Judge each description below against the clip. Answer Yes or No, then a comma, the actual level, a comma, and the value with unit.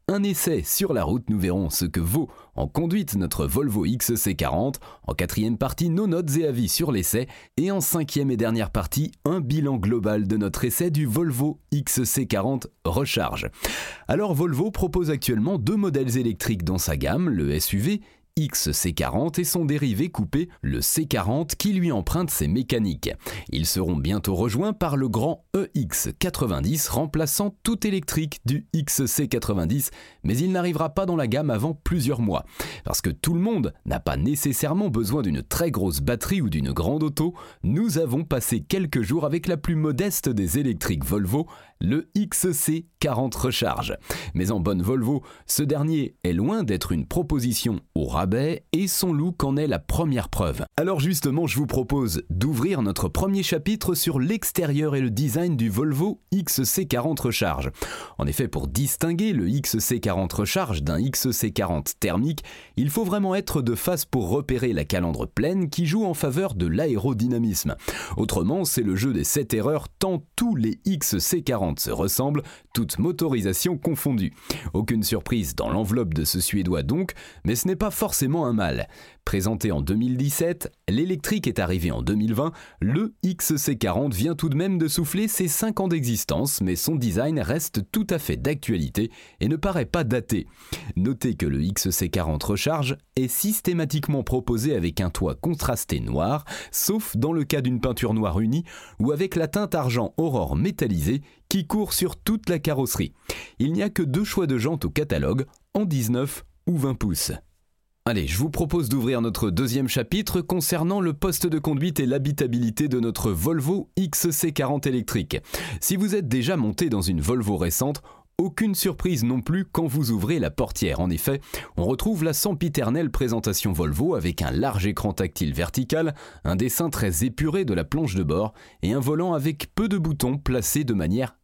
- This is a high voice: No, medium, 140 Hz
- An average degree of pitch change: No, wide, 7.5 semitones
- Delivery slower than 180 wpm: Yes, average, 170 wpm